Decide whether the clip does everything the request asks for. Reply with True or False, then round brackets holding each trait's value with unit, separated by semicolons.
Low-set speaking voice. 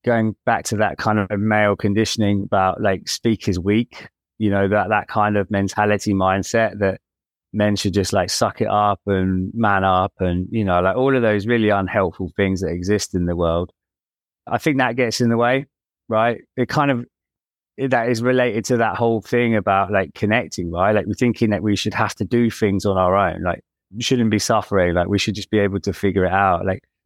True (105 Hz)